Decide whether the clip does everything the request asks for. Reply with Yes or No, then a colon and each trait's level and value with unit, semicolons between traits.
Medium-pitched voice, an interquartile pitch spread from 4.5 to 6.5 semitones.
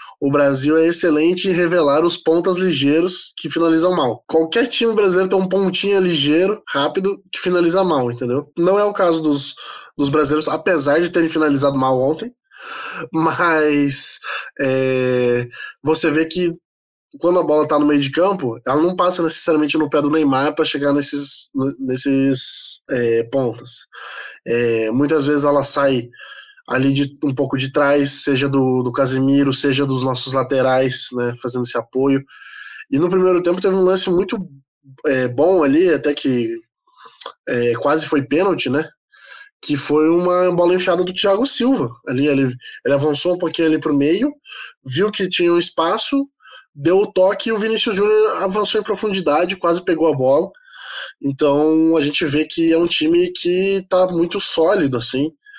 Yes: medium, 155 Hz; average, 4.9 semitones